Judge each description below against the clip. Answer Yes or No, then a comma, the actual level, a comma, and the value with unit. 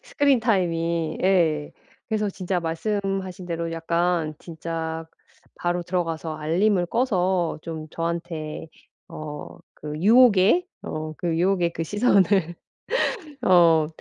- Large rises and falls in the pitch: No, average, 2.9 semitones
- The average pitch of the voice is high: No, medium, 175 Hz